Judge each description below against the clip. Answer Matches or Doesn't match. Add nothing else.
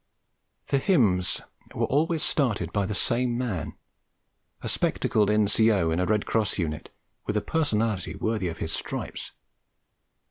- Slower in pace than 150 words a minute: Matches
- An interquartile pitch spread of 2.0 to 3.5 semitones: Doesn't match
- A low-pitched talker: Matches